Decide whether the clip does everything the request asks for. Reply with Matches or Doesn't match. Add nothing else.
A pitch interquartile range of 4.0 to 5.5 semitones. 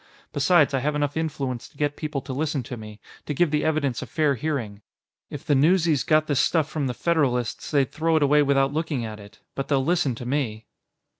Doesn't match